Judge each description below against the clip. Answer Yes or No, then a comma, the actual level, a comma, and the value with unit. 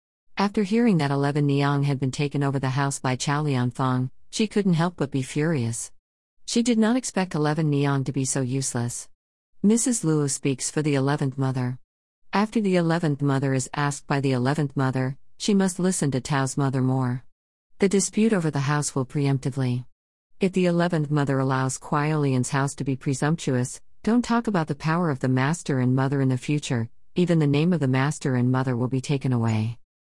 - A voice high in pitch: No, medium, 140 Hz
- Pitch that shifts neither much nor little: Yes, average, 3.5 semitones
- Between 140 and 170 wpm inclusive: No, average, 190 wpm